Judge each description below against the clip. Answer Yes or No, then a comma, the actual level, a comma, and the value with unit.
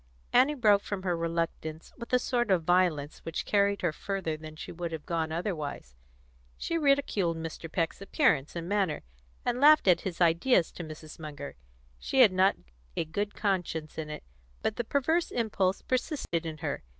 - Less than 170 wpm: No, average, 175 wpm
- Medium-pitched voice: Yes, medium, 175 Hz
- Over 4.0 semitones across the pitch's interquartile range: Yes, average, 4.6 semitones